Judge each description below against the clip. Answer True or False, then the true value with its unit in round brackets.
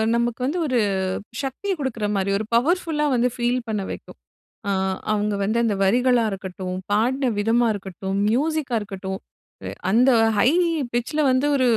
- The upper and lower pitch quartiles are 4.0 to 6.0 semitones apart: True (4.3 semitones)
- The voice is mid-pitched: False (235 Hz)